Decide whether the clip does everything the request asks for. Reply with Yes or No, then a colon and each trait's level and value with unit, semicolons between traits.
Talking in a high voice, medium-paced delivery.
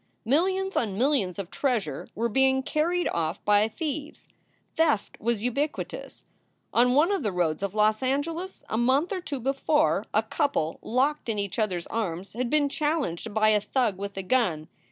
Yes: high, 245 Hz; average, 175 wpm